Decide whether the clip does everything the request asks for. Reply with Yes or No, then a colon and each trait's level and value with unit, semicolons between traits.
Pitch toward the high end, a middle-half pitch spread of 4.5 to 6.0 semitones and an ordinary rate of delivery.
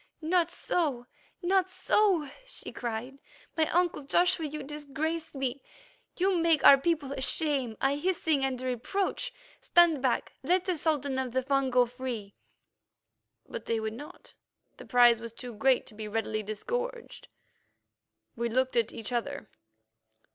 Yes: very high, 275 Hz; average, 5.3 semitones; average, 150 wpm